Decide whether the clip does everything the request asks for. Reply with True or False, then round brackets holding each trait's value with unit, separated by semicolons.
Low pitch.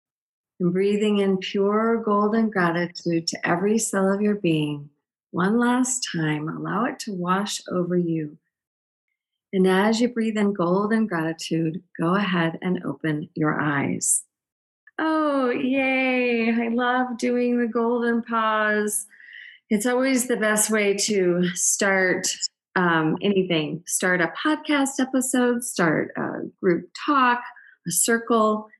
False (210 Hz)